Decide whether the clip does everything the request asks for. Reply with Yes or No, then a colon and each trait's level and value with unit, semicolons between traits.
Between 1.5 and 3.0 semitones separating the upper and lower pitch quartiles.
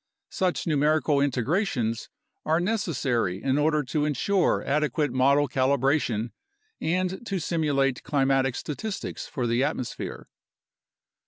No: average, 3.6 semitones